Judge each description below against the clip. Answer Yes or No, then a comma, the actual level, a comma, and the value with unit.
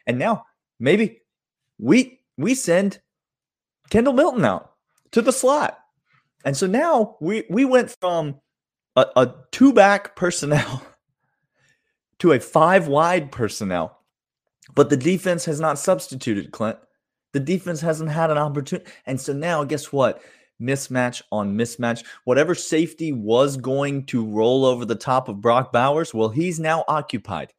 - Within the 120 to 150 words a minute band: Yes, average, 140 wpm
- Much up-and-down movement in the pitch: Yes, wide, 5.8 semitones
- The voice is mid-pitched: Yes, medium, 150 Hz